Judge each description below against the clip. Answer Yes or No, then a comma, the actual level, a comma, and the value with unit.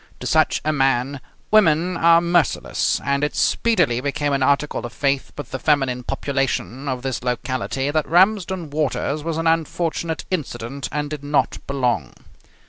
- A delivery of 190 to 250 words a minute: No, average, 155 wpm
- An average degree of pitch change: Yes, average, 3.5 semitones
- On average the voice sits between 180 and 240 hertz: No, medium, 145 Hz